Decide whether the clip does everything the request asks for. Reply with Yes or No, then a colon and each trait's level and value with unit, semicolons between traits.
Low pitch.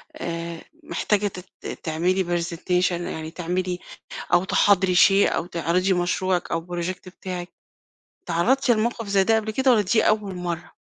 No: medium, 185 Hz